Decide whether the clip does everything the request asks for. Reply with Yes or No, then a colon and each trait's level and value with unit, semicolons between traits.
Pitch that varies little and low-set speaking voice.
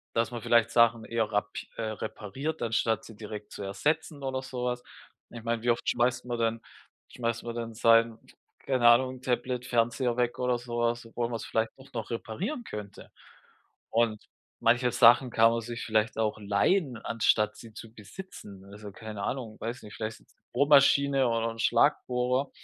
Yes: narrow, 1.9 semitones; low, 115 Hz